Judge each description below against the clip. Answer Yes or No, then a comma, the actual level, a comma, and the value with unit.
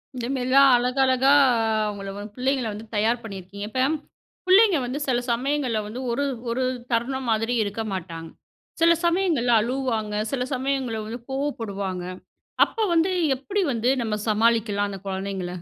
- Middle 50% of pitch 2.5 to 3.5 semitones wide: No, average, 4.3 semitones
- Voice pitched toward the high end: Yes, high, 240 Hz